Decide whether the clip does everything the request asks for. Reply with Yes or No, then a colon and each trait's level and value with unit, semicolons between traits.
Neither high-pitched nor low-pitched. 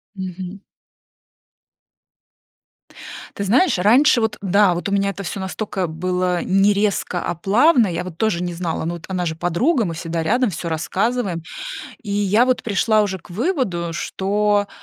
No: high, 195 Hz